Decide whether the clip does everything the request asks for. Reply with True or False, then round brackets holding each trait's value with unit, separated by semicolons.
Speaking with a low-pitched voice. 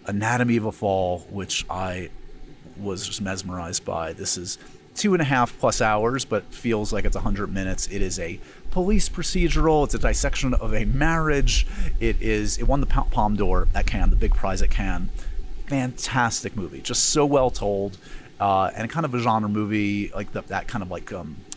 True (105 Hz)